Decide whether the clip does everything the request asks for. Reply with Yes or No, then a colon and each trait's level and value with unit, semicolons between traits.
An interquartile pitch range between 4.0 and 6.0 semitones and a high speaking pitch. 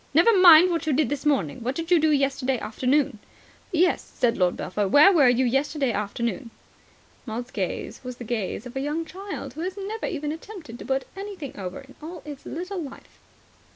Yes: average, 5.3 semitones; very high, 280 Hz